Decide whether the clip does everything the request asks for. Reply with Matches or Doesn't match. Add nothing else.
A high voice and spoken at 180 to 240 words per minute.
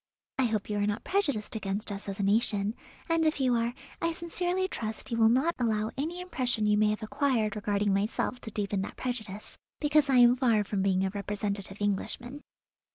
Matches